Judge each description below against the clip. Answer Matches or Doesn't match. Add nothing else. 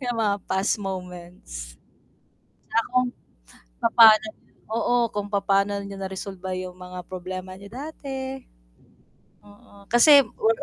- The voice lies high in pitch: Matches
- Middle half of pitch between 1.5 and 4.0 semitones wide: Matches